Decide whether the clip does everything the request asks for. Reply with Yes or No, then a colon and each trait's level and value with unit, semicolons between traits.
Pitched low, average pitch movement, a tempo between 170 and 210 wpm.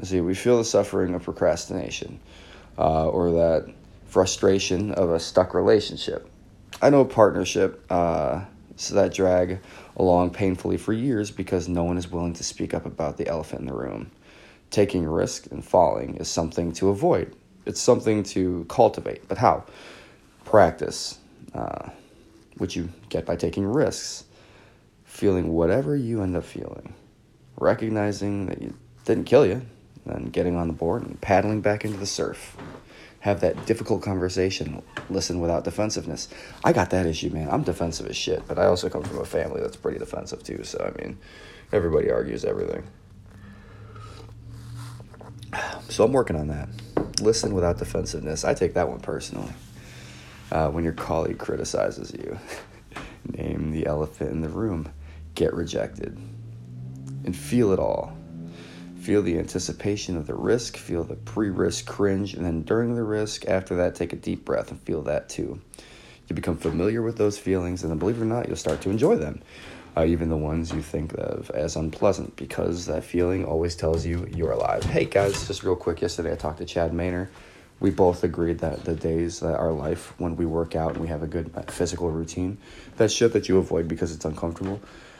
Yes: very low, 90 Hz; average, 4.1 semitones; average, 175 wpm